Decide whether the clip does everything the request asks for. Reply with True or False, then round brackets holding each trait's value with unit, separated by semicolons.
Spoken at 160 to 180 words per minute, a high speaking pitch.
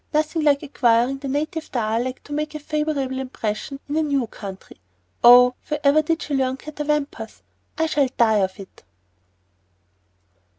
False (145 wpm; 280 Hz)